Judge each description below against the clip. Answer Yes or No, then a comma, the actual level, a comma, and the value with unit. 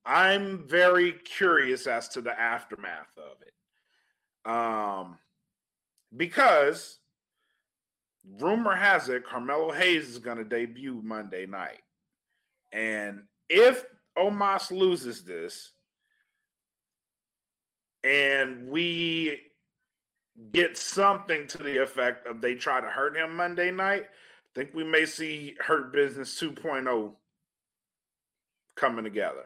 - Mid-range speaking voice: Yes, medium, 160 Hz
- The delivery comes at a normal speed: No, slow, 105 wpm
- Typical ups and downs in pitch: No, wide, 7.4 semitones